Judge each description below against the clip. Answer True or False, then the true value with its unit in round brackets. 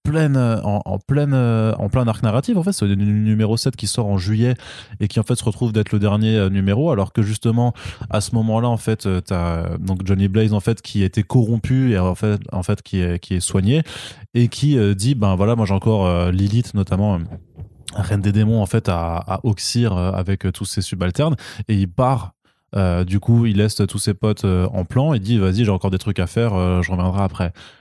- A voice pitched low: True (105 Hz)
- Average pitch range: True (3.3 semitones)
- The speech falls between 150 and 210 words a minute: False (220 wpm)